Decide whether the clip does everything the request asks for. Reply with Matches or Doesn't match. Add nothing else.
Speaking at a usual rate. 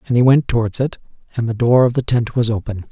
Doesn't match